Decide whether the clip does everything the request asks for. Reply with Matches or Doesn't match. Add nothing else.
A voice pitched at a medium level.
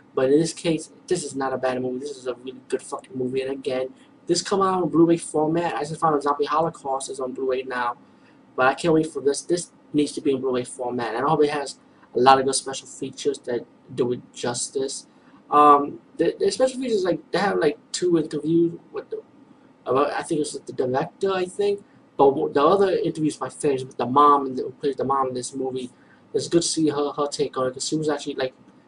Matches